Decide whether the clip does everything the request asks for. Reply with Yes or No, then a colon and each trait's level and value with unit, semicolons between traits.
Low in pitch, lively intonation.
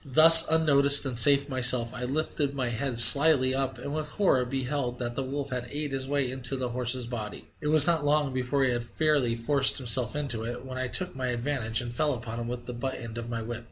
No: low, 130 Hz; average, 2.9 semitones